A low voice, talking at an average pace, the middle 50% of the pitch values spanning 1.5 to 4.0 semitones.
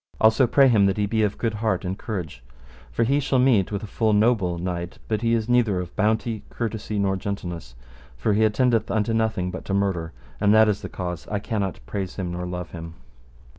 No: low, 105 Hz; fast, 215 wpm; average, 3.5 semitones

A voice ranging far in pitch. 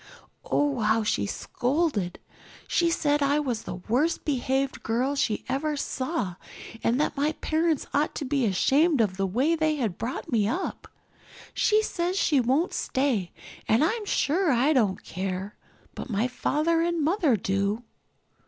Yes: wide, 6.0 semitones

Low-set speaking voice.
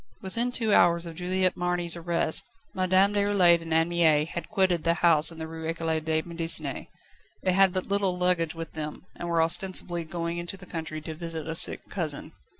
No: medium, 170 Hz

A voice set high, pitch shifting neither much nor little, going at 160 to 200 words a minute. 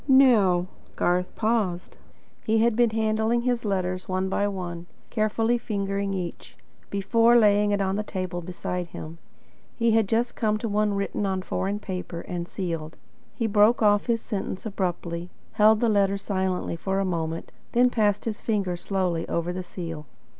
Yes: high, 200 Hz; average, 3.3 semitones; average, 170 wpm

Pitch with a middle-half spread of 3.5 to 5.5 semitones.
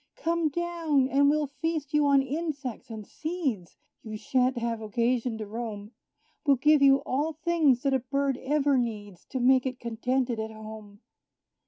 Yes: average, 4.3 semitones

